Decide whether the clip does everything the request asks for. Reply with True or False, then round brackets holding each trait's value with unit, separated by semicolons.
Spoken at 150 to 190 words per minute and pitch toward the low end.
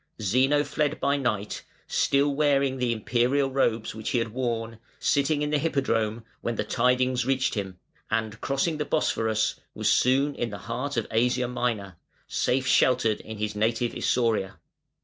True (160 wpm; 125 Hz)